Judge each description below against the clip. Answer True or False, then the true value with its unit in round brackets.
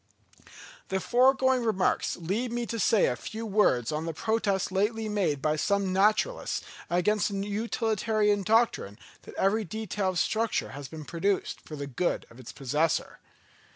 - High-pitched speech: True (200 Hz)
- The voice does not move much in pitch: False (5.0 semitones)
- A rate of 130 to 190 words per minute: True (160 wpm)